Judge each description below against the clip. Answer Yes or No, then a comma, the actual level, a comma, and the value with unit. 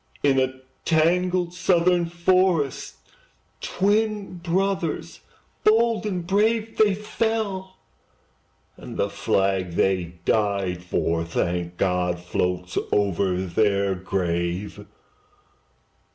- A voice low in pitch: No, medium, 145 Hz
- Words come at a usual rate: No, slow, 90 wpm